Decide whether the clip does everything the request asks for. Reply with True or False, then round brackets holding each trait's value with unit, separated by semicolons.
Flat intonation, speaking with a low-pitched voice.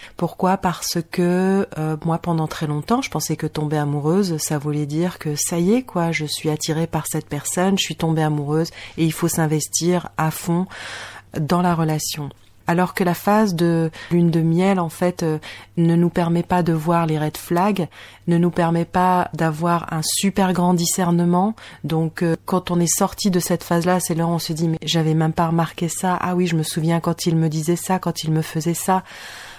False (2.0 semitones; 170 Hz)